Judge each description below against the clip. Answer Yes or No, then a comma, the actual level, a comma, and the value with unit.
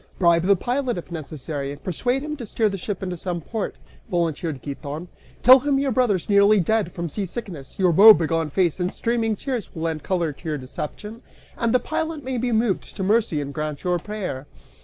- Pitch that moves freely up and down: Yes, wide, 6.0 semitones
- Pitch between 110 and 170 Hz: No, medium, 185 Hz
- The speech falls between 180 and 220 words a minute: Yes, average, 200 wpm